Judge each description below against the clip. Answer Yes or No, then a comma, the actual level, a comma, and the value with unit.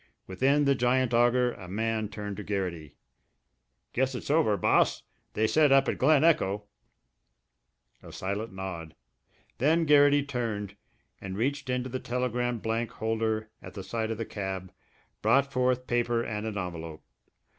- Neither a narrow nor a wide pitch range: Yes, average, 4.2 semitones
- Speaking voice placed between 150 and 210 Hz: No, low, 115 Hz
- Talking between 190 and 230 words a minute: No, average, 155 wpm